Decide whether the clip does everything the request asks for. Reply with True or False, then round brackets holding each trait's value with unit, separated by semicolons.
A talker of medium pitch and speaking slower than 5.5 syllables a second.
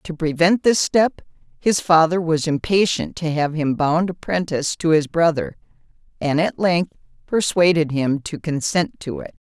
True (165 Hz; 4.6 syllables/s)